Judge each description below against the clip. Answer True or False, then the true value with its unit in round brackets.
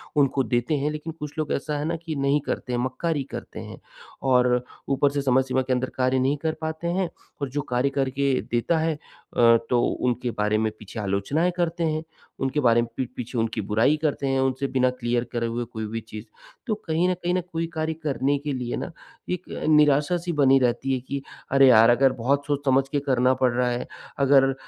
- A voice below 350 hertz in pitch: True (135 Hz)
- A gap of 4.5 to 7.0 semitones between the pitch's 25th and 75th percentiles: False (3.3 semitones)